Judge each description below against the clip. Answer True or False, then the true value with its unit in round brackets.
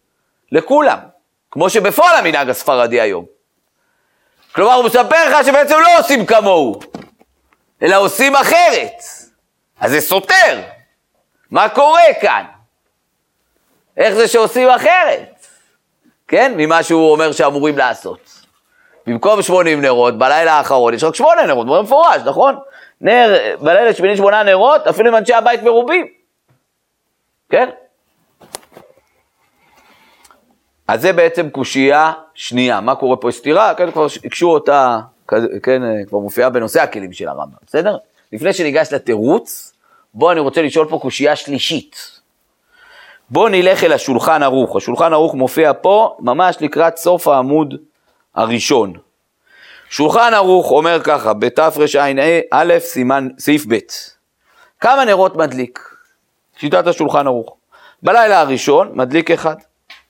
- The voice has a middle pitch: True (165 Hz)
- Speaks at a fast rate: False (120 wpm)